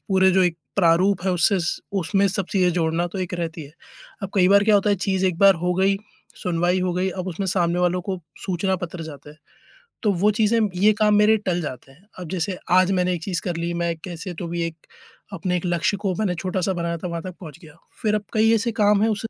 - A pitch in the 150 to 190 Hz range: Yes, medium, 185 Hz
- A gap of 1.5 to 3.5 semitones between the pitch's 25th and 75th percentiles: Yes, narrow, 2.6 semitones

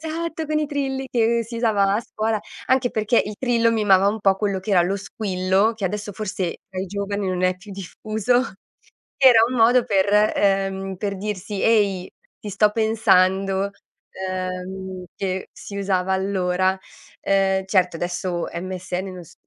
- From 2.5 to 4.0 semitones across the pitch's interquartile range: Yes, average, 2.8 semitones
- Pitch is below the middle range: No, high, 200 Hz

